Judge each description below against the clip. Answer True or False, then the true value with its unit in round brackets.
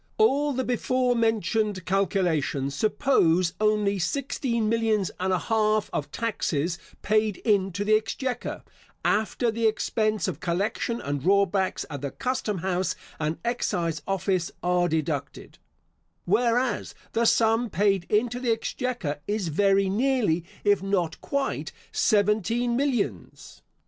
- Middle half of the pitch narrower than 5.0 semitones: True (4.4 semitones)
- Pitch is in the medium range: False (210 Hz)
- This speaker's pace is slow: True (125 wpm)